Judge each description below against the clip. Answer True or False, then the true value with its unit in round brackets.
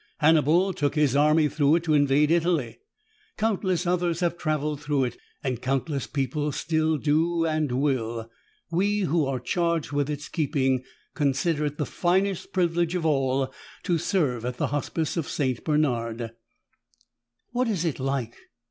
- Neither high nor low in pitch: True (150 Hz)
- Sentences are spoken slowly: False (155 wpm)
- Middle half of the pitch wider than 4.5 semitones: False (3.8 semitones)